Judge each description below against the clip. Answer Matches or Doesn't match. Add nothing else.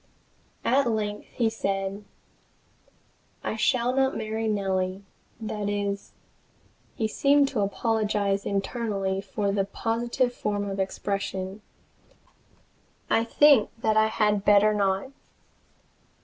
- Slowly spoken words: Matches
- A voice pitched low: Doesn't match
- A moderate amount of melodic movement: Doesn't match